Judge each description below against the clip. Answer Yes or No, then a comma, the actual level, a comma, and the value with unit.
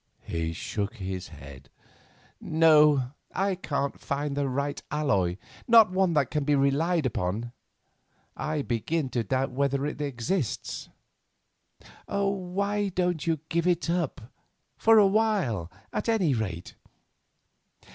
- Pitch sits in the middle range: Yes, medium, 145 Hz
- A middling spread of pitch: No, wide, 6.8 semitones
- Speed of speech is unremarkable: No, slow, 115 wpm